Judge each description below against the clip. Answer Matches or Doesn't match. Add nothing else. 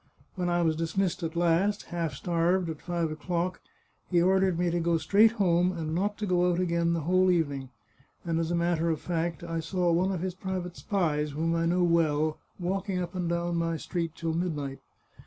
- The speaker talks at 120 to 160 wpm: Doesn't match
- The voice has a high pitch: Doesn't match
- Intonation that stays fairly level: Matches